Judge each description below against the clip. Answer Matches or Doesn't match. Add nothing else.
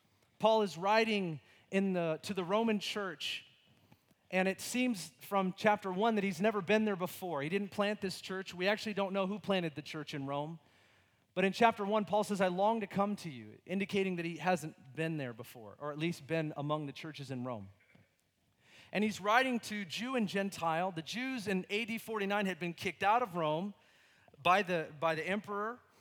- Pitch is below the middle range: Doesn't match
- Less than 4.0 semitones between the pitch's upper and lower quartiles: Doesn't match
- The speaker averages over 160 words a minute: Matches